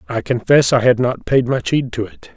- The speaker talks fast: Yes, fast, 255 wpm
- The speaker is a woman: No, male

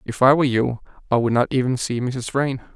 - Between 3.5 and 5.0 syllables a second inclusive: No, 5.8 syllables/s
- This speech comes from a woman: No, male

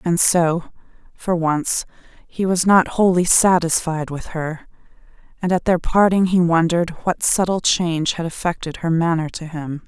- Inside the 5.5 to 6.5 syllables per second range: No, 4.5 syllables/s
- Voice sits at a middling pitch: Yes, medium, 170 Hz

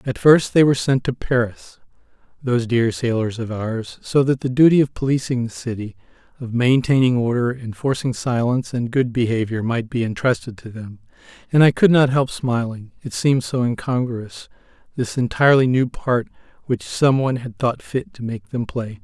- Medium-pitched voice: No, low, 125 Hz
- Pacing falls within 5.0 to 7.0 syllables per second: Yes, 5.1 syllables/s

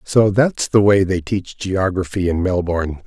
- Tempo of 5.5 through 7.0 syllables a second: No, 4.4 syllables/s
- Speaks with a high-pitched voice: No, very low, 95 Hz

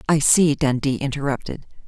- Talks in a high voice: No, medium, 140 Hz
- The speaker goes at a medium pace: No, slow, 130 wpm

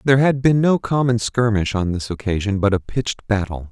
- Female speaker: No, male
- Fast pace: Yes, fast, 210 wpm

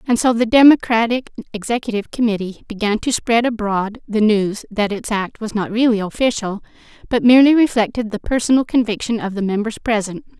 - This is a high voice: Yes, high, 225 Hz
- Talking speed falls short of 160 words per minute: No, average, 165 wpm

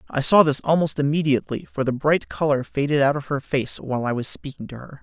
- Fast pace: Yes, fast, 240 wpm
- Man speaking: Yes, male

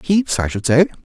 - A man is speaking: Yes, male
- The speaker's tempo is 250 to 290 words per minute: No, fast, 215 wpm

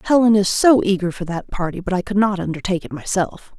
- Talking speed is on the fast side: Yes, fast, 235 wpm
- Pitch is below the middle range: No, high, 190 Hz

